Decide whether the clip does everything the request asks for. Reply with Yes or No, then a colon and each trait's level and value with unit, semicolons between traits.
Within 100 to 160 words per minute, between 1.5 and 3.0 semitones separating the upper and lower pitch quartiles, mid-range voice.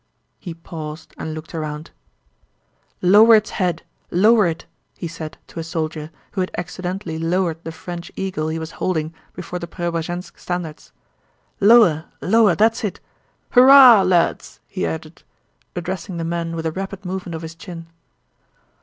Yes: average, 150 wpm; average, 2.7 semitones; medium, 175 Hz